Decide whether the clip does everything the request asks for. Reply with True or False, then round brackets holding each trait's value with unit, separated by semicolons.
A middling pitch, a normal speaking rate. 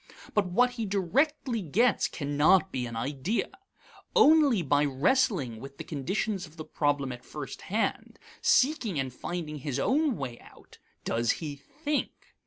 True (175 Hz; 150 wpm)